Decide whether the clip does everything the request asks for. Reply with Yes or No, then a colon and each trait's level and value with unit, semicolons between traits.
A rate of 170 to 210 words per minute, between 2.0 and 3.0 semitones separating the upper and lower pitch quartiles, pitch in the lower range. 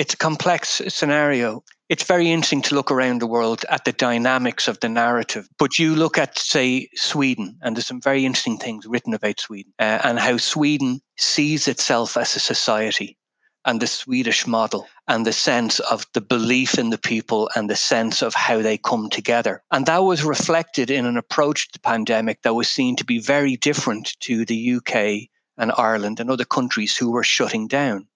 No: average, 195 wpm; average, 4.2 semitones; low, 130 Hz